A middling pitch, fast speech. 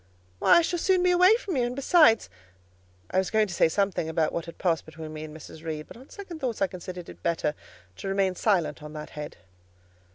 Yes: medium, 175 Hz; fast, 225 wpm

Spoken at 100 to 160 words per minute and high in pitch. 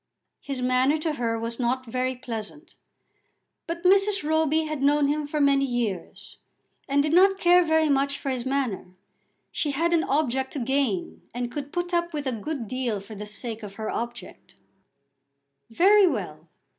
No: average, 170 wpm; very high, 275 Hz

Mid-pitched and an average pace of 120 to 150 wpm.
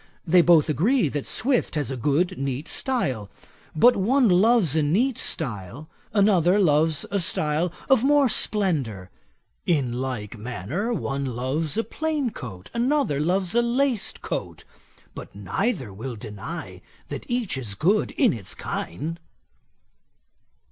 Yes: medium, 160 Hz; slow, 135 wpm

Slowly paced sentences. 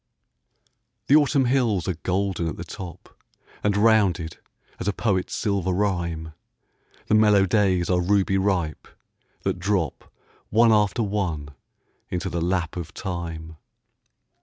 Yes: slow, 130 wpm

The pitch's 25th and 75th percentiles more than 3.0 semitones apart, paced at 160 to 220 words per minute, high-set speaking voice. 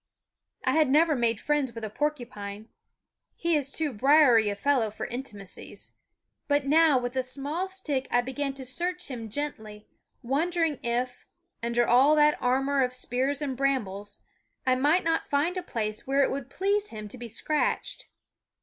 Yes: average, 3.9 semitones; average, 165 wpm; very high, 265 Hz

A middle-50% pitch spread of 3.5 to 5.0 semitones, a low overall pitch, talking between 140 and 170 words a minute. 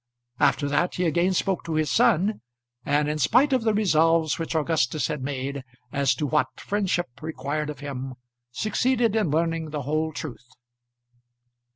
No: average, 4.1 semitones; medium, 155 Hz; average, 160 wpm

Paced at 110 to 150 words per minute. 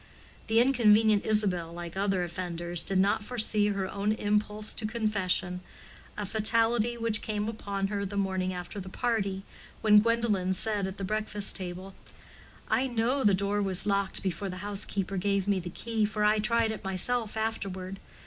No: average, 170 wpm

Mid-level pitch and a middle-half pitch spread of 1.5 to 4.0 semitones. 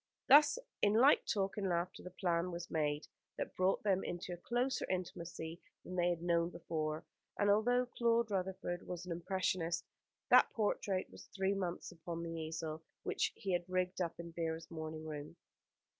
Yes: medium, 175 Hz; average, 2.7 semitones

